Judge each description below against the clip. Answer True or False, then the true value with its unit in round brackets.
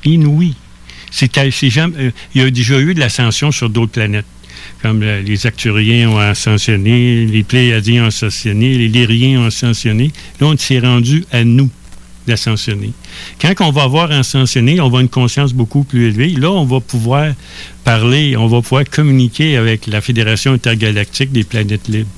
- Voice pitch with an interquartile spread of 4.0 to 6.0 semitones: False (3.5 semitones)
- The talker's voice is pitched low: True (120 Hz)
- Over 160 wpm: True (175 wpm)